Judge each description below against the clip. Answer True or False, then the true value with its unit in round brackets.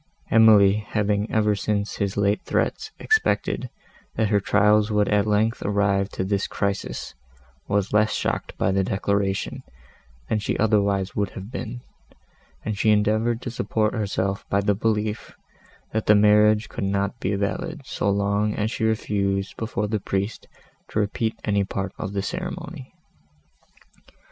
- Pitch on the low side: True (105 Hz)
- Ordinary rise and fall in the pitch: False (1.4 semitones)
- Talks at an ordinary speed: True (150 wpm)